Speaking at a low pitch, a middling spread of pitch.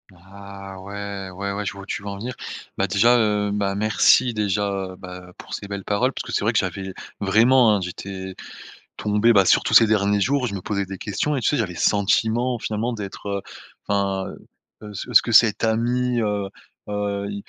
No: low, 100 Hz; narrow, 2.2 semitones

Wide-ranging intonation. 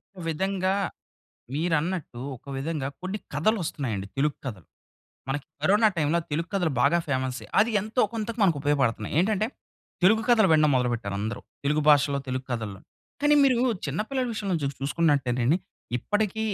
Yes: wide, 6.6 semitones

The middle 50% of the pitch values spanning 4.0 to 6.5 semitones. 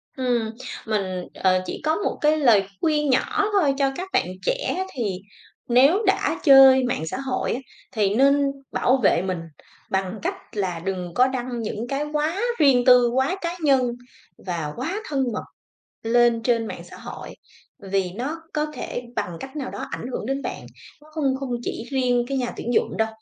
Yes: average, 4.6 semitones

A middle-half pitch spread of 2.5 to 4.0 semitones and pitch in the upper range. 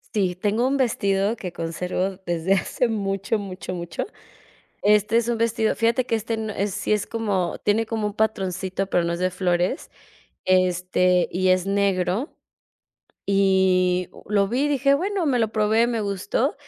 Yes: average, 3.5 semitones; high, 200 Hz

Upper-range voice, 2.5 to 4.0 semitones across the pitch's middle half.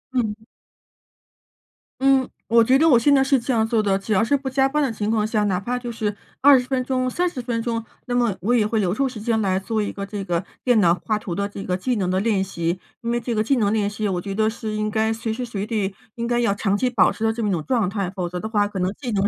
Yes: high, 220 Hz; average, 3.5 semitones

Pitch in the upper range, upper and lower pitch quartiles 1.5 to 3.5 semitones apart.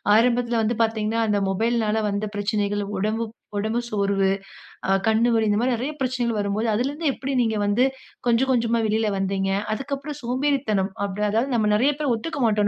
Yes: high, 225 Hz; average, 2.9 semitones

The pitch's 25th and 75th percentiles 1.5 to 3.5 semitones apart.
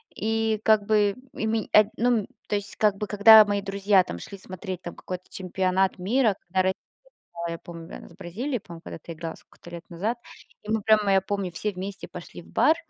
Yes: average, 2.8 semitones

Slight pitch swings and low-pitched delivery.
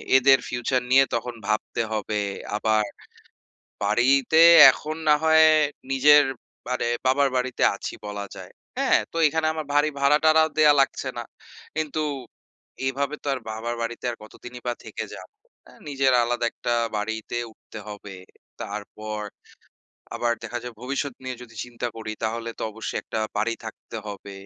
No: average, 4.0 semitones; low, 120 Hz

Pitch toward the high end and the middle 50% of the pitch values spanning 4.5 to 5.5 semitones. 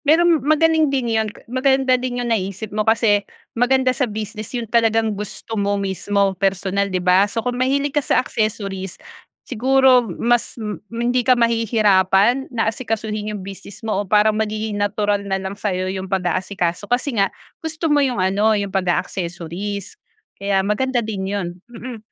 No: high, 215 Hz; average, 3.8 semitones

